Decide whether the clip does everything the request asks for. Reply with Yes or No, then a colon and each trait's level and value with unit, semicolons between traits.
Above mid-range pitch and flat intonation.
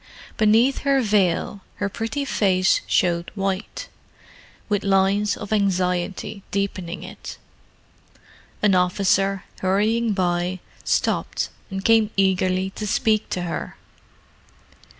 Yes: high, 195 Hz; narrow, 2.3 semitones